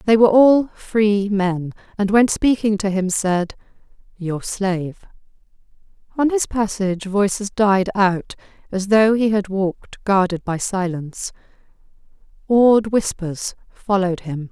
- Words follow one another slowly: Yes, slow, 130 wpm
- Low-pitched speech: No, high, 200 Hz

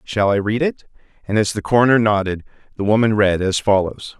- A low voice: Yes, low, 105 Hz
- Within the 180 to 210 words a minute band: Yes, average, 200 wpm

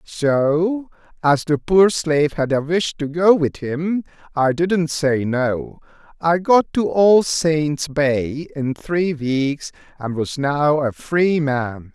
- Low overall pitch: No, medium, 155 Hz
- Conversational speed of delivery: Yes, average, 160 wpm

